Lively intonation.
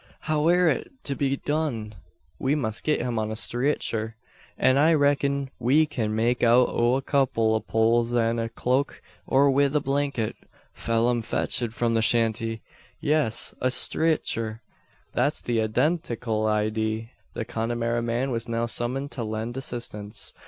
No: average, 3.5 semitones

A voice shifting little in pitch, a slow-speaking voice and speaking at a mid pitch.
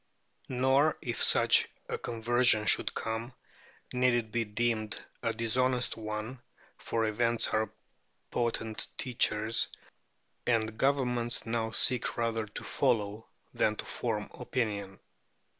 No: narrow, 2.0 semitones; slow, 115 wpm; low, 115 Hz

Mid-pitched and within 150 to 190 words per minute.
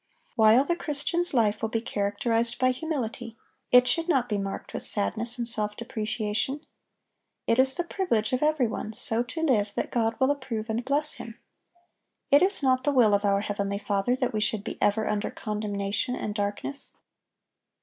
No: high, 230 Hz; average, 185 wpm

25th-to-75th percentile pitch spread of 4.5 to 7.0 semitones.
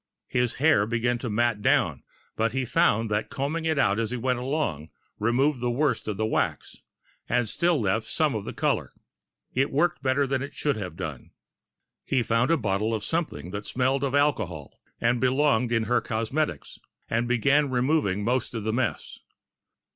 No: average, 4.0 semitones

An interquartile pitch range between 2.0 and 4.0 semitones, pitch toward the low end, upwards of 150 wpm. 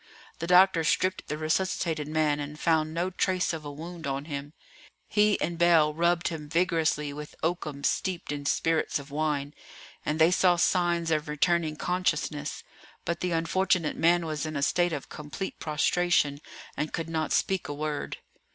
No: narrow, 2.5 semitones; medium, 160 Hz; average, 170 wpm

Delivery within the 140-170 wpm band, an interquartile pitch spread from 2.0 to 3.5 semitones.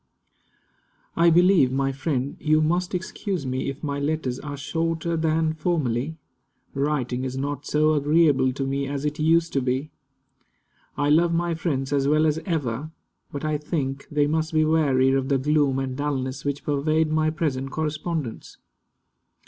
Yes: average, 160 wpm; average, 2.8 semitones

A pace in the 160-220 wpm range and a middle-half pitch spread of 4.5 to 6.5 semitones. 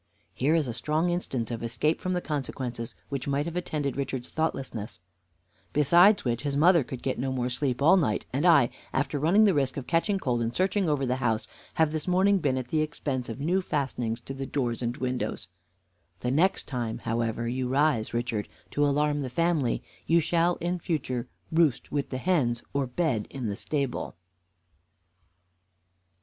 Yes: average, 185 wpm; average, 4.8 semitones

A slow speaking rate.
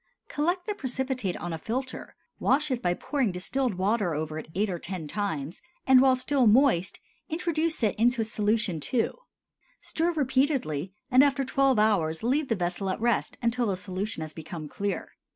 No: average, 170 wpm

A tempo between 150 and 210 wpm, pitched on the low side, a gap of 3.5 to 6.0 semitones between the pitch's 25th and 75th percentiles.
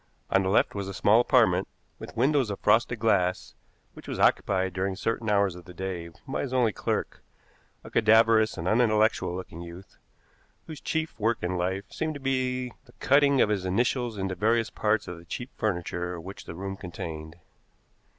Yes: average, 180 wpm; low, 105 Hz; average, 4.4 semitones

